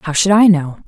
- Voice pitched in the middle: Yes, medium, 180 Hz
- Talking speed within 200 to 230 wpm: No, fast, 275 wpm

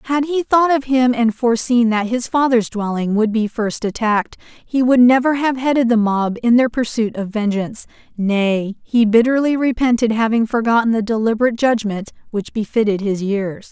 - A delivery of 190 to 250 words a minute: No, average, 175 wpm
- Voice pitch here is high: Yes, high, 230 Hz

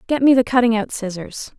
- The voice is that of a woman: Yes, female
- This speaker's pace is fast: Yes, fast, 225 wpm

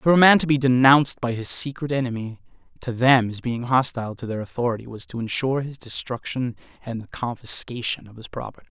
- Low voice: Yes, low, 125 Hz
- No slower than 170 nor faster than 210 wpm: Yes, average, 200 wpm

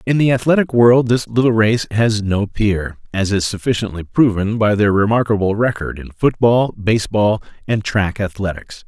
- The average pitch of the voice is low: Yes, low, 110 Hz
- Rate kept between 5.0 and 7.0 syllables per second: No, 4.8 syllables/s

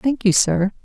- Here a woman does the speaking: Yes, female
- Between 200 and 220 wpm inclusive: Yes, fast, 215 wpm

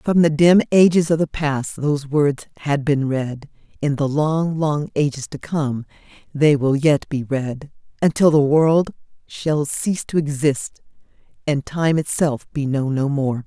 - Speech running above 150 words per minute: Yes, average, 170 wpm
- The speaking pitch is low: No, medium, 145 Hz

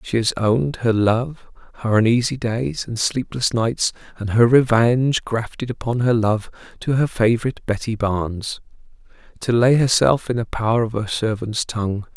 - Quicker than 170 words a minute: No, average, 160 wpm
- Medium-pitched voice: No, low, 115 Hz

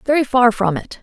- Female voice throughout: Yes, female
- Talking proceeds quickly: Yes, fast, 235 wpm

